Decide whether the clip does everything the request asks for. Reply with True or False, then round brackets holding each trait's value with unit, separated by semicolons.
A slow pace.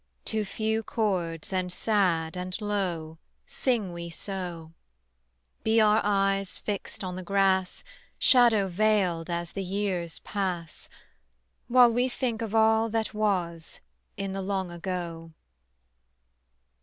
True (120 wpm)